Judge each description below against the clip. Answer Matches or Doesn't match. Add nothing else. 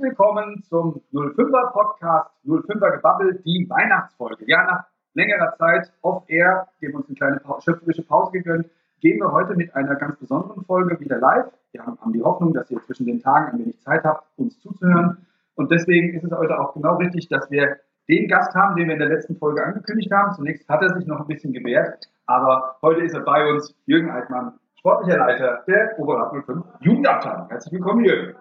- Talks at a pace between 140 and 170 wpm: Doesn't match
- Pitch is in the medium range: Matches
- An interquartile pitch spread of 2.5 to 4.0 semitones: Doesn't match